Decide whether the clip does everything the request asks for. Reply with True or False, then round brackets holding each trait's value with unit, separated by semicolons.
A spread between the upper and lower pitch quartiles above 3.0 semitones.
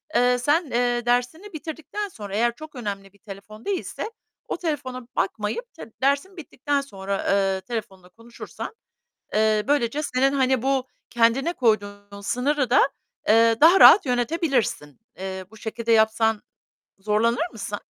True (5.1 semitones)